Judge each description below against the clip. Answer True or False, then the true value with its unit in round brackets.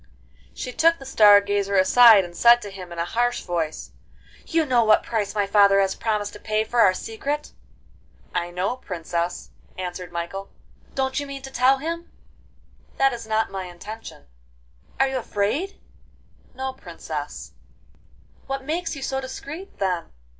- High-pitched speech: True (220 Hz)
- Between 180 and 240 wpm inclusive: False (160 wpm)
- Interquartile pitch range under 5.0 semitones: False (5.6 semitones)